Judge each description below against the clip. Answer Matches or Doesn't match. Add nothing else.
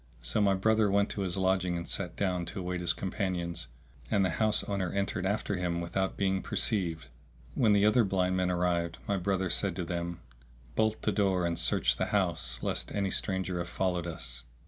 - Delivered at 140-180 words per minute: Doesn't match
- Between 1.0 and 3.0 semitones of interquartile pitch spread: Matches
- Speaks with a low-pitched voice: Matches